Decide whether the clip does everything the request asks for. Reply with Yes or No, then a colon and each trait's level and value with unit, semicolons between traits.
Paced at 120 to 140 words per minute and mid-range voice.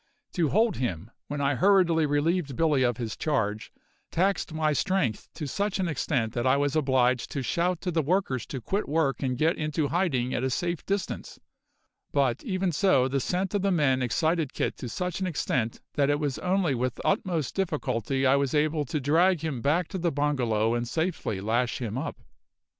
No: average, 195 wpm; medium, 145 Hz